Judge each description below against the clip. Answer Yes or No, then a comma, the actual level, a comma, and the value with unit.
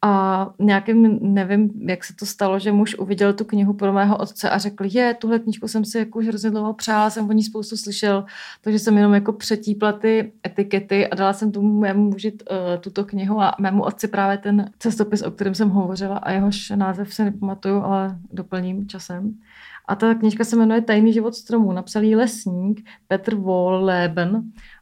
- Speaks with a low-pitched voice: No, high, 205 Hz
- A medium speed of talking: No, fast, 185 wpm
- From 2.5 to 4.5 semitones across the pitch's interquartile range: No, narrow, 1.8 semitones